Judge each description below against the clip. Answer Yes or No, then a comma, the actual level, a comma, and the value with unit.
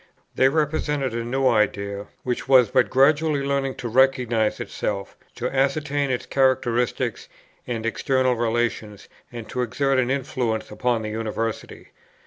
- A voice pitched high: No, low, 125 Hz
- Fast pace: No, slow, 135 wpm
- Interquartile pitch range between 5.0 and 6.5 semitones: No, average, 3.0 semitones